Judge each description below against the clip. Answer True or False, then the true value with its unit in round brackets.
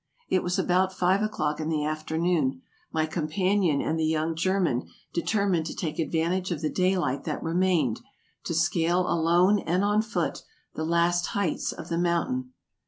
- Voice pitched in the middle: True (170 Hz)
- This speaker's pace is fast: False (165 wpm)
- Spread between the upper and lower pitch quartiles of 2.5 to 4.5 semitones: True (2.9 semitones)